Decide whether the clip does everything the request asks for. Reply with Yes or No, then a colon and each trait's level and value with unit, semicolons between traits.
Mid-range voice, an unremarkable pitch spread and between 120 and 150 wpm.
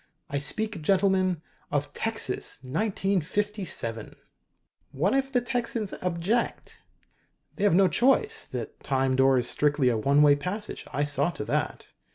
No: medium, 180 Hz; wide, 6.7 semitones; average, 140 wpm